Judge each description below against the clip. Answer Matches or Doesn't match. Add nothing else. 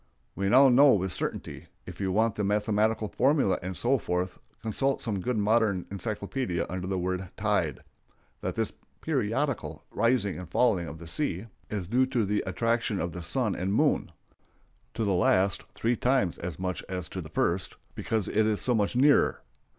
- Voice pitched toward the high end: Doesn't match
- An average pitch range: Matches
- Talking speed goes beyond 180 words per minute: Doesn't match